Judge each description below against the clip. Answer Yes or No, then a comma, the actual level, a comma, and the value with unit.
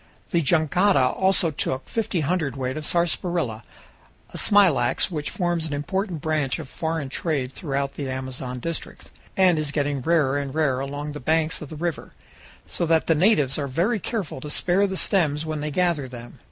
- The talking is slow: No, average, 180 wpm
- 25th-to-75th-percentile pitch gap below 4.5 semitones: Yes, average, 4.0 semitones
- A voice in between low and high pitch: Yes, medium, 155 Hz